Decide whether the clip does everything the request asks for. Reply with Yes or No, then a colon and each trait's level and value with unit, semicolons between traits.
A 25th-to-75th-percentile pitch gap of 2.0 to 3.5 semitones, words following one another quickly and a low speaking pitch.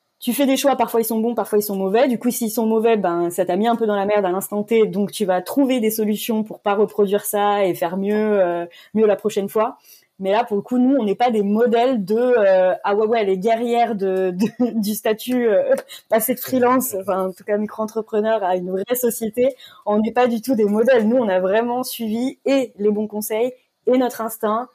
No: average, 2.8 semitones; fast, 245 wpm; high, 220 Hz